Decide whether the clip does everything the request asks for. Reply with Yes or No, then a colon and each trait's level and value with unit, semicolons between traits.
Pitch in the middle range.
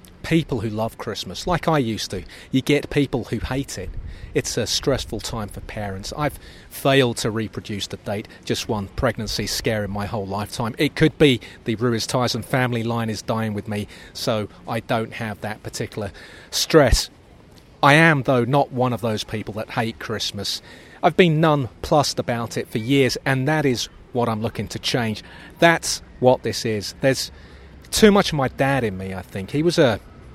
No: low, 115 Hz